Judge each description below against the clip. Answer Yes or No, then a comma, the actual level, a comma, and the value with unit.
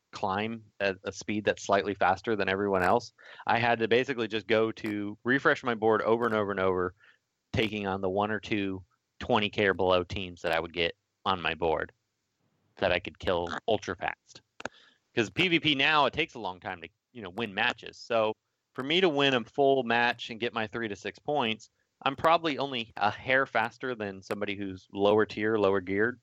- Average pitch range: Yes, average, 3.4 semitones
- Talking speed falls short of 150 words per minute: No, fast, 205 wpm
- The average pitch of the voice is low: Yes, low, 110 Hz